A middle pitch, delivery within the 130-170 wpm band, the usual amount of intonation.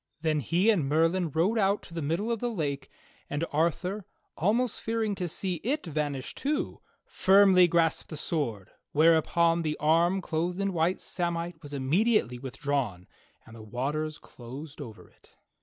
Yes: medium, 165 Hz; average, 155 wpm; average, 4.6 semitones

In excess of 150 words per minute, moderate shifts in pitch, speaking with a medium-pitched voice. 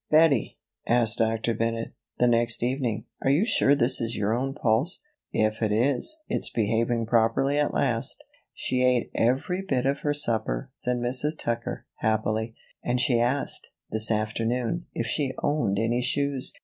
No: average, 160 wpm; average, 3.3 semitones; low, 120 Hz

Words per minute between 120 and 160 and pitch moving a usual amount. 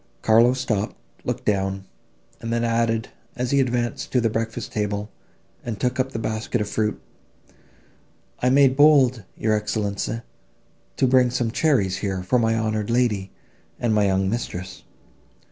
Yes: average, 150 wpm; average, 3.0 semitones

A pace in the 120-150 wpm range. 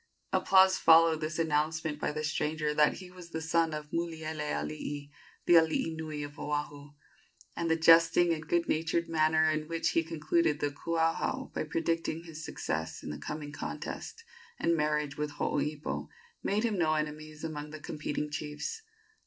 No: average, 160 wpm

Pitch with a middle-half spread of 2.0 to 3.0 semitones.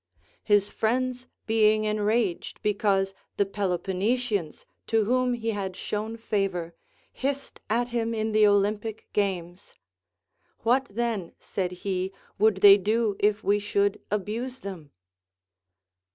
Yes: narrow, 2.5 semitones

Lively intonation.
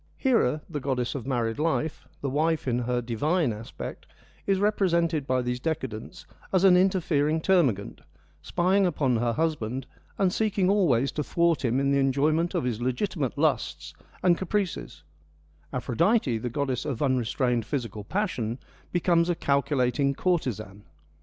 Yes: wide, 5.8 semitones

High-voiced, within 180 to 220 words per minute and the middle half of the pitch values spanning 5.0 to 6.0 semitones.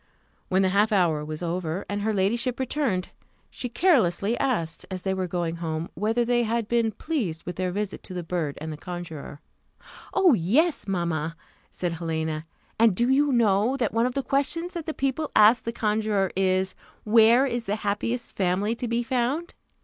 Yes: high, 205 Hz; average, 185 wpm; average, 5.3 semitones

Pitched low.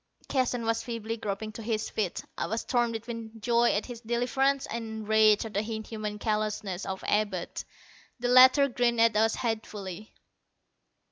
No: high, 225 Hz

